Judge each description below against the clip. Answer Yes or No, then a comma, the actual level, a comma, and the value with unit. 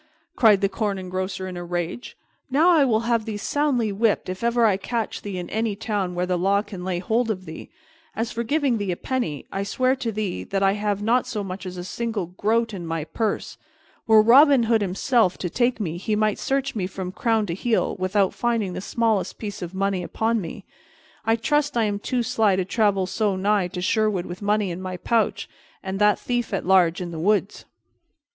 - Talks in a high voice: Yes, high, 205 Hz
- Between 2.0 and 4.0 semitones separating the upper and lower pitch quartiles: Yes, average, 3.6 semitones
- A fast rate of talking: Yes, fast, 215 wpm